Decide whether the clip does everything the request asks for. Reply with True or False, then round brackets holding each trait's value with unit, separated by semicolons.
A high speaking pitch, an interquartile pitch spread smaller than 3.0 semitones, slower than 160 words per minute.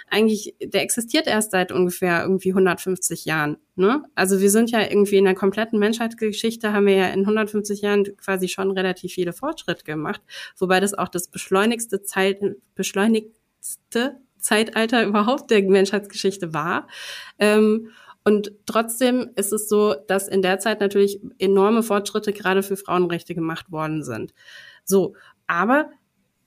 True (200 Hz; 2.4 semitones; 145 wpm)